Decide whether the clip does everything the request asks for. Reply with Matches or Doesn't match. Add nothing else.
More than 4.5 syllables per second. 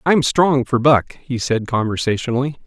Matches